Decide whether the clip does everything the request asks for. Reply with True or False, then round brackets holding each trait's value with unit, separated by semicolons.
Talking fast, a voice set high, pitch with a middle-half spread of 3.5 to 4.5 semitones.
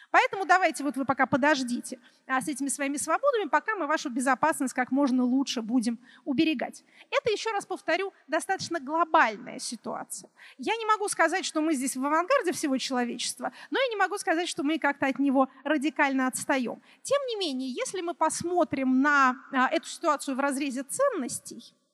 True (165 wpm; 290 Hz; 4.1 semitones)